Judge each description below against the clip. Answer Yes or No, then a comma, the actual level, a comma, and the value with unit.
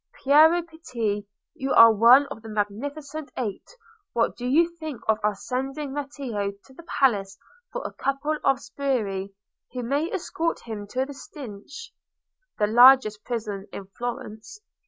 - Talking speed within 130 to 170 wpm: Yes, average, 150 wpm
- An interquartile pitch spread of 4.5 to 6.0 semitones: Yes, average, 5.2 semitones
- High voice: Yes, very high, 255 Hz